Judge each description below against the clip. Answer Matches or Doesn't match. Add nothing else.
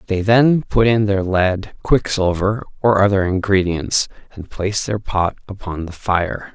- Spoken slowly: Doesn't match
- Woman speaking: Doesn't match